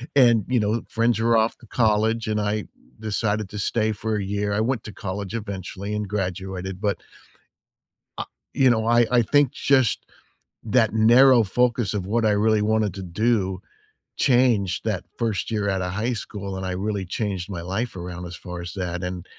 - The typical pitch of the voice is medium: No, low, 105 Hz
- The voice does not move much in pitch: No, average, 3.1 semitones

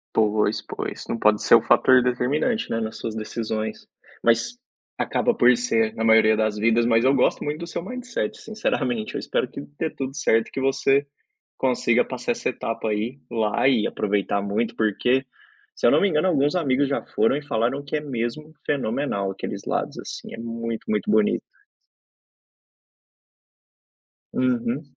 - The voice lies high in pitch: No, low, 120 Hz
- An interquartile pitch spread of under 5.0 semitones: Yes, average, 4.5 semitones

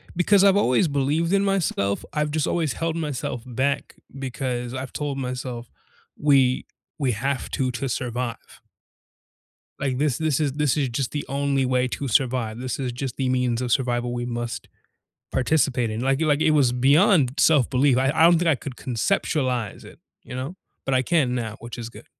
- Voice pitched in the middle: No, low, 130 Hz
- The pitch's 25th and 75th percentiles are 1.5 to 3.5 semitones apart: Yes, average, 3.2 semitones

